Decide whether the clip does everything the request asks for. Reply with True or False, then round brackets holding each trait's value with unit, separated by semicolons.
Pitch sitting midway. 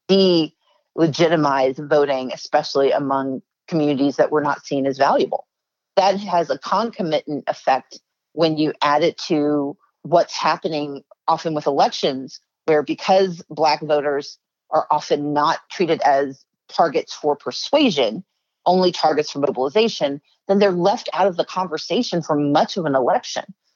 True (155 Hz)